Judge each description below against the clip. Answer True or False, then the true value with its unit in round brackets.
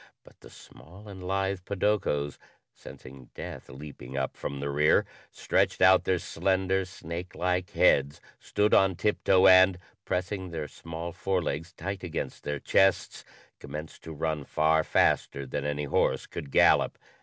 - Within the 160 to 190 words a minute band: False (145 wpm)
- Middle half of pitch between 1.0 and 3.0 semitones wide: False (4.4 semitones)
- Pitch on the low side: True (85 Hz)